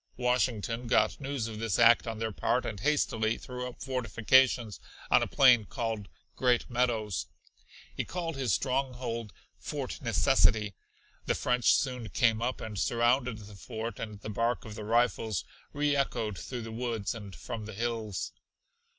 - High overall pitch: No, low, 115 Hz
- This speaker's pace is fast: No, average, 155 wpm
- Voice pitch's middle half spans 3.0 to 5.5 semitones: No, narrow, 2.6 semitones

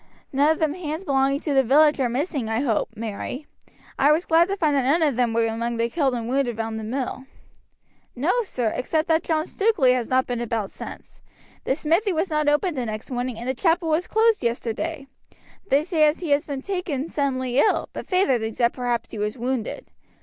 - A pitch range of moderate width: Yes, average, 4.9 semitones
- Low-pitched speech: No, very high, 275 Hz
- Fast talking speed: Yes, fast, 215 wpm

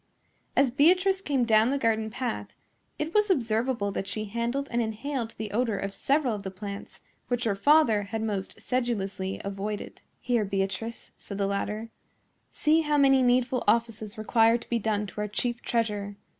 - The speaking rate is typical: Yes, average, 170 wpm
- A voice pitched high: Yes, high, 225 Hz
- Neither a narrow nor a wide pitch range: Yes, average, 3.7 semitones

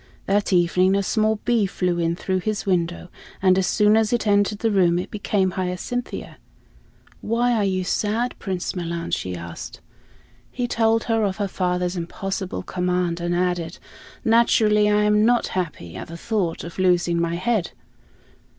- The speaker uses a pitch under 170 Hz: No, high, 190 Hz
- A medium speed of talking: Yes, average, 165 wpm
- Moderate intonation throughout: Yes, average, 3.3 semitones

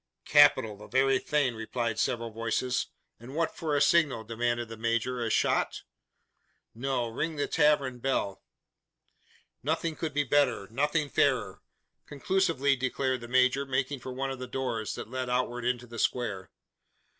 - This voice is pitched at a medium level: No, low, 130 Hz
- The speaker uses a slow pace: No, average, 155 wpm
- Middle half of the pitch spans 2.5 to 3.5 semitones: Yes, average, 3.1 semitones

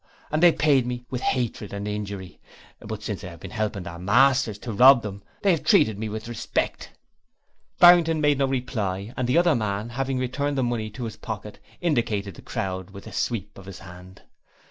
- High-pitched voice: No, low, 115 Hz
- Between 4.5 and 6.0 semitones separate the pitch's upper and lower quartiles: Yes, average, 4.9 semitones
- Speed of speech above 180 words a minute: Yes, average, 200 wpm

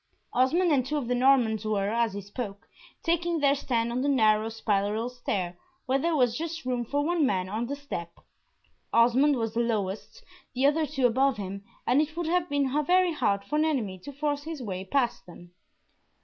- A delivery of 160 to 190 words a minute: No, average, 200 wpm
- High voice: Yes, very high, 250 Hz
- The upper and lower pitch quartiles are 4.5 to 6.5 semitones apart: Yes, average, 5.1 semitones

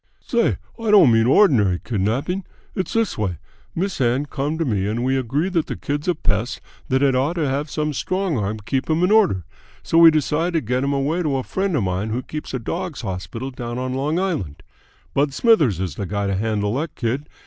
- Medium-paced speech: No, fast, 220 wpm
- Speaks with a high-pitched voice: No, low, 135 Hz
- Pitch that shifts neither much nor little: No, wide, 6.6 semitones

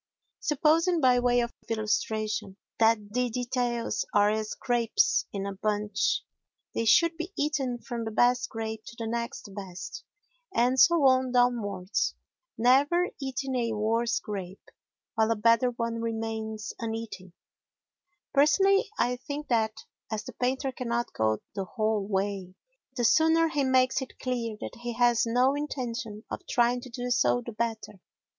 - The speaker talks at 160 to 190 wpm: No, average, 150 wpm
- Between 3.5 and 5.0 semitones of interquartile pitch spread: No, average, 2.8 semitones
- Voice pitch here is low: No, high, 235 Hz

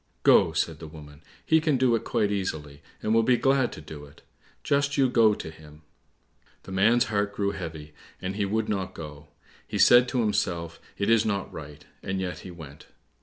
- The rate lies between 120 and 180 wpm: No, average, 200 wpm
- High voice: No, low, 100 Hz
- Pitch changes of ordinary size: No, wide, 6.6 semitones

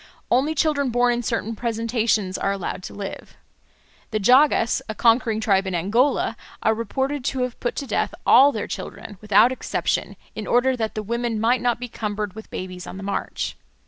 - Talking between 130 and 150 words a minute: No, average, 185 wpm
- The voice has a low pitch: No, high, 230 Hz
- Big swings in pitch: No, average, 3.0 semitones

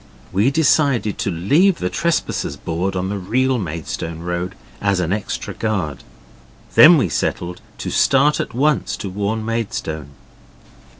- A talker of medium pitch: No, low, 100 Hz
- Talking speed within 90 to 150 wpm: Yes, average, 140 wpm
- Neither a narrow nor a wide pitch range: No, wide, 6.8 semitones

